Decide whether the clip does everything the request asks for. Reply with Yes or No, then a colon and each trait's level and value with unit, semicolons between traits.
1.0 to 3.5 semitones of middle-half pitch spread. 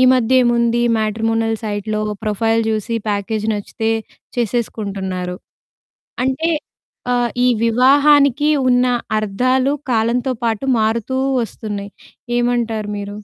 Yes: average, 2.7 semitones